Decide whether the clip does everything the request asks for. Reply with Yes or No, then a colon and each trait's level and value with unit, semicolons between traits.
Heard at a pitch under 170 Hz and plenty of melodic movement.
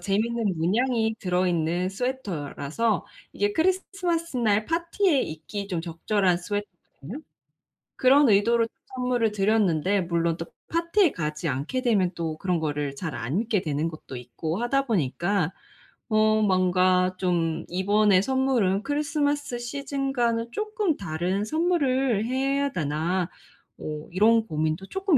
No: high, 205 Hz; wide, 7.2 semitones